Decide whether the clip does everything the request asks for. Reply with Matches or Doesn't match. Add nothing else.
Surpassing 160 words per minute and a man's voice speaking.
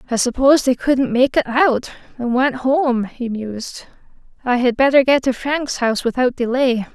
Doesn't match